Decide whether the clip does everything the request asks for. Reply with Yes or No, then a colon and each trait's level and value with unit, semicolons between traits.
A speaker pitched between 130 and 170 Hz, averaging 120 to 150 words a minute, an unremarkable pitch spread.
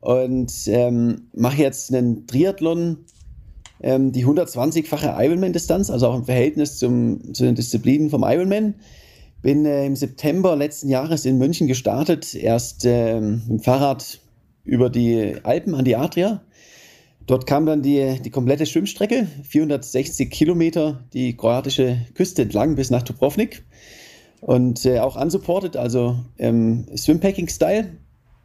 Yes: low, 135 Hz; average, 135 wpm; average, 4.4 semitones